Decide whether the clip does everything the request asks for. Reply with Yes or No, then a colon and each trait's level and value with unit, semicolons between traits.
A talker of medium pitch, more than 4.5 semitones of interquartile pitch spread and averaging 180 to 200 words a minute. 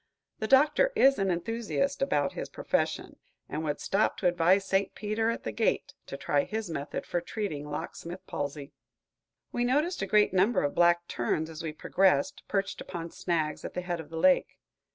Yes: medium, 180 Hz; wide, 5.4 semitones; average, 185 wpm